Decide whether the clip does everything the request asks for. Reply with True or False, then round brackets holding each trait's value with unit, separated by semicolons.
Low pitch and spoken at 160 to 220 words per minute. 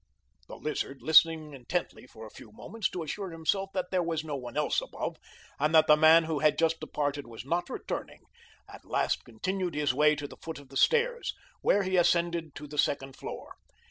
False (155 Hz; 205 wpm)